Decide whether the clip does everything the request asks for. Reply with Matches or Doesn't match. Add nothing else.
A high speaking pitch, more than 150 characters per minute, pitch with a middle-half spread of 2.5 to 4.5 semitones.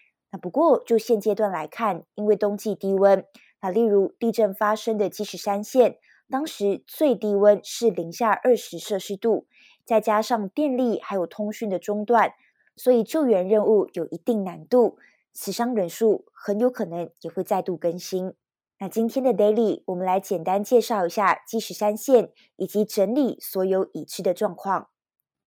Matches